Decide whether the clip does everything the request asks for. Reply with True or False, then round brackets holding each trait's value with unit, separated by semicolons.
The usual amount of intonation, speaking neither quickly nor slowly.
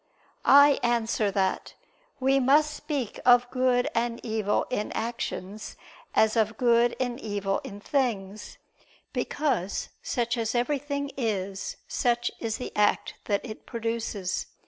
False (3.2 semitones; 125 wpm)